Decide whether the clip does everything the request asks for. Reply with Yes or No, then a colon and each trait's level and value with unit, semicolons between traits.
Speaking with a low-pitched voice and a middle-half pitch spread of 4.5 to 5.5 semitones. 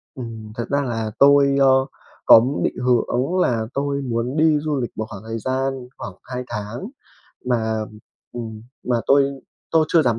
No: low, 125 Hz; average, 3.5 semitones